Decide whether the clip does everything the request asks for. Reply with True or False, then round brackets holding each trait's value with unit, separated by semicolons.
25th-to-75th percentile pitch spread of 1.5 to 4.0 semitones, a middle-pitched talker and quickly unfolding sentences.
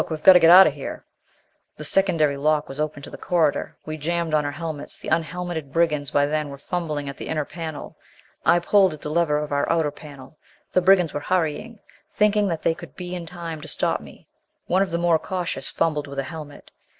True (2.8 semitones; 160 Hz; 220 wpm)